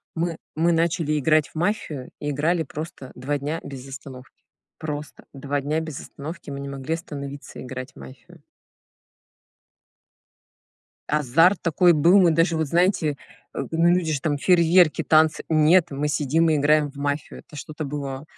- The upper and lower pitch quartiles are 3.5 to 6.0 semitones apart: No, average, 2.8 semitones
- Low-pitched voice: No, medium, 150 Hz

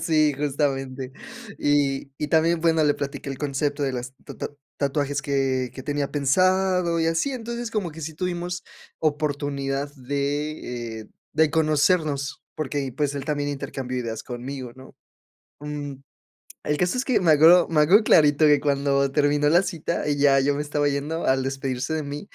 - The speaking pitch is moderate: Yes, medium, 145 Hz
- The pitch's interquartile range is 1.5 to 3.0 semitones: Yes, narrow, 2.5 semitones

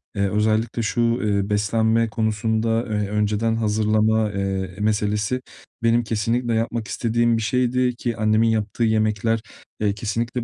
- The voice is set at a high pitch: No, low, 110 Hz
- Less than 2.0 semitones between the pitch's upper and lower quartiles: Yes, narrow, 1.6 semitones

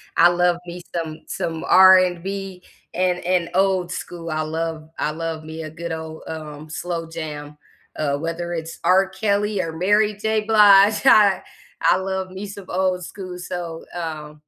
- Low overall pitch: No, medium, 175 Hz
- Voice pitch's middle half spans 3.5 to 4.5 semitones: No, average, 2.9 semitones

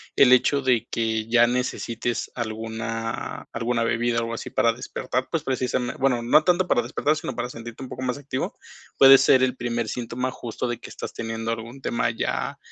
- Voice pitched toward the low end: Yes, low, 120 Hz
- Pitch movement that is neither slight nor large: No, narrow, 2.0 semitones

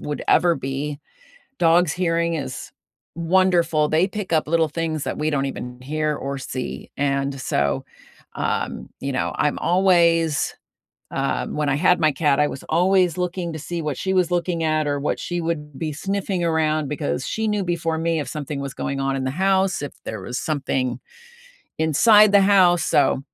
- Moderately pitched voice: Yes, medium, 160 Hz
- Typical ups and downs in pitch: Yes, average, 3.8 semitones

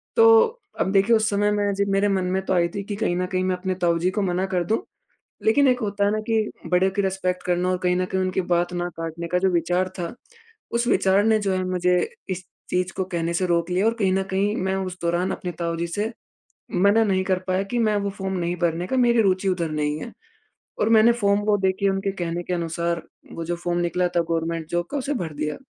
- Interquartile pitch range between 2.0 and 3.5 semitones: Yes, narrow, 2.6 semitones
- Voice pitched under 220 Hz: Yes, medium, 185 Hz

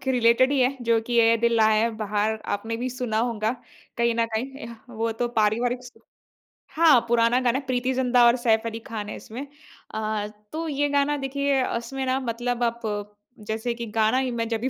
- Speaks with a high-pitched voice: Yes, high, 235 Hz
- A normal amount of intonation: No, narrow, 2.3 semitones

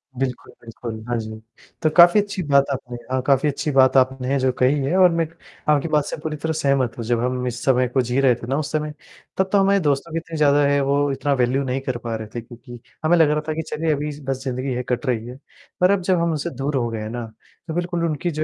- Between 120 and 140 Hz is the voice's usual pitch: Yes, low, 135 Hz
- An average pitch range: Yes, average, 3.9 semitones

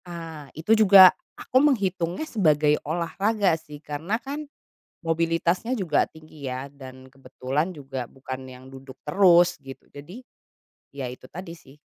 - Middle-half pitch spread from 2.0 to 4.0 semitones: No, wide, 5.6 semitones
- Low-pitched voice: No, medium, 160 Hz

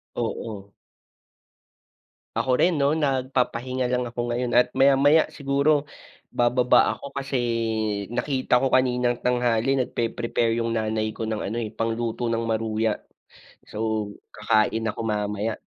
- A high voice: No, low, 120 Hz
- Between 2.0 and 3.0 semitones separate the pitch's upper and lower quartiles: Yes, narrow, 2.6 semitones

